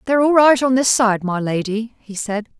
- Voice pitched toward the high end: Yes, high, 230 Hz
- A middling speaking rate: No, fast, 230 wpm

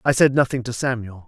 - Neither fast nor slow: No, fast, 235 wpm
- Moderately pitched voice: No, low, 125 Hz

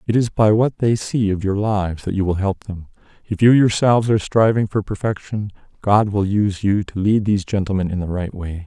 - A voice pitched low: Yes, low, 100 Hz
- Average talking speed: No, fast, 230 wpm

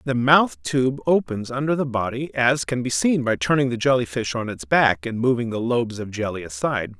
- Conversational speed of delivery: No, fast, 225 wpm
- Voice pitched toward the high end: No, low, 120 Hz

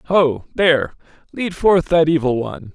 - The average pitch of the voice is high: No, medium, 150 Hz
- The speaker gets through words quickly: No, average, 155 wpm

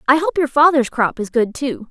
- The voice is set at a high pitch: Yes, very high, 275 Hz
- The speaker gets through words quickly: Yes, fast, 250 wpm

